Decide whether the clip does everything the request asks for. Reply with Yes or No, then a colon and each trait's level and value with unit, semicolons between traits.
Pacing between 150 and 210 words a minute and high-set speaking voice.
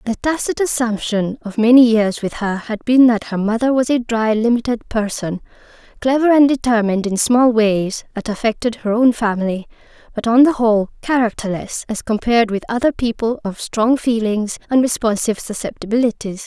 Yes: average, 165 wpm; high, 230 Hz